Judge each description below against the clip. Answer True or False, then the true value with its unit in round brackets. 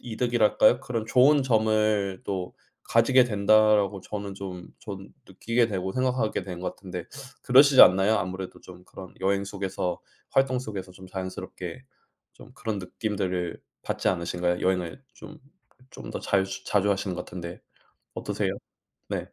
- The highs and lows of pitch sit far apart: False (3.2 semitones)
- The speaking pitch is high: False (100 Hz)